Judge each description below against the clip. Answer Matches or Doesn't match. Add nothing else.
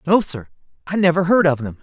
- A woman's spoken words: Doesn't match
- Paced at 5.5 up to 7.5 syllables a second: Matches